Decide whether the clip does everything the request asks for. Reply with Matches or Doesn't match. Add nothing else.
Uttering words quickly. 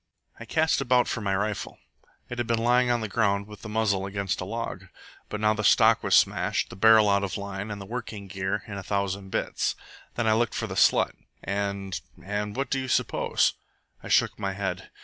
Matches